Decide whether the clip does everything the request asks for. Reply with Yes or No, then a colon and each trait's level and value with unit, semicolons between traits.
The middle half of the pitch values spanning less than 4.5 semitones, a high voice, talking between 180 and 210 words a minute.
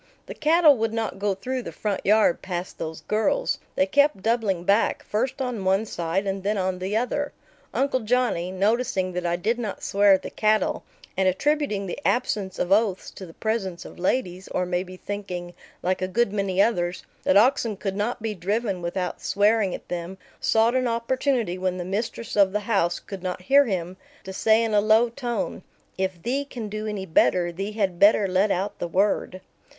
Yes: average, 3.6 semitones; high, 200 Hz; average, 195 wpm